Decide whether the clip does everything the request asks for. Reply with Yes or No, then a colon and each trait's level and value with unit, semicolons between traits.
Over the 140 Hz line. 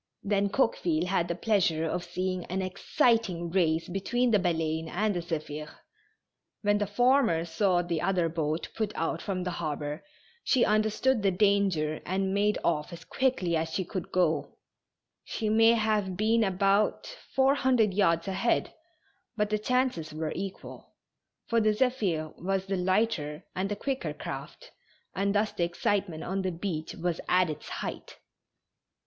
Yes: high, 190 Hz